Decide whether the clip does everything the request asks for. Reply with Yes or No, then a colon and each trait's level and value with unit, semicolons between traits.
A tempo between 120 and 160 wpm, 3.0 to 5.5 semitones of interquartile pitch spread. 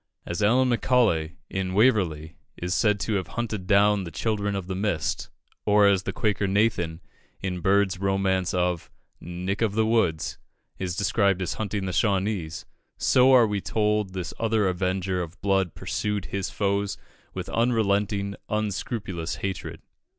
No: average, 150 wpm; narrow, 2.6 semitones